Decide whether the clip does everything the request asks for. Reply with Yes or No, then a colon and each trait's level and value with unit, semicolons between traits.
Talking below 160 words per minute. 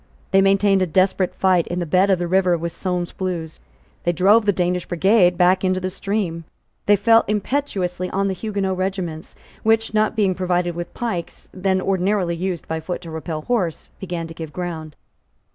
No: average, 185 wpm